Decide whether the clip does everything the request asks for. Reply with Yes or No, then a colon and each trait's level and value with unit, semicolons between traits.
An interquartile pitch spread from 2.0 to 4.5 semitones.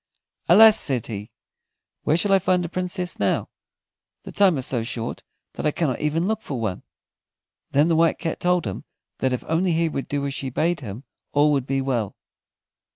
No: wide, 5.4 semitones